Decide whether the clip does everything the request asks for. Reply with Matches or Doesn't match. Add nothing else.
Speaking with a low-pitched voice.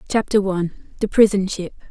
Doesn't match